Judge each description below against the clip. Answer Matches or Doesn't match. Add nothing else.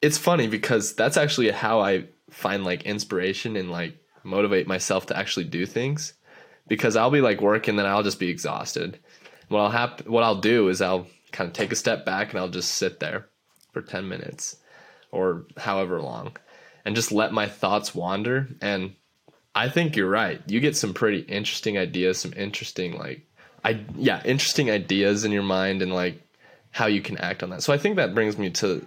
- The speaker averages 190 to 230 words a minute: Matches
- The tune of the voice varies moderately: Matches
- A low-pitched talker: Matches